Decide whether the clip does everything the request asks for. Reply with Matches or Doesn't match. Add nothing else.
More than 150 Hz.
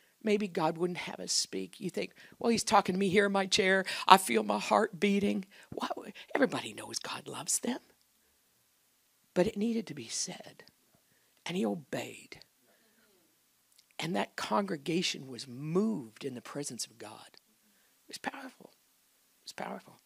Matches